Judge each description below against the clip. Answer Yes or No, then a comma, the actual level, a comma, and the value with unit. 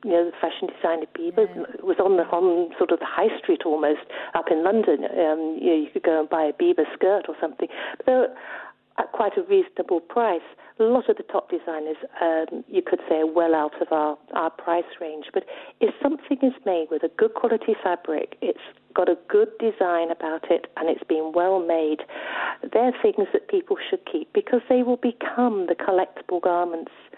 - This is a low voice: No, high, 200 Hz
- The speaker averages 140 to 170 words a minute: No, fast, 205 wpm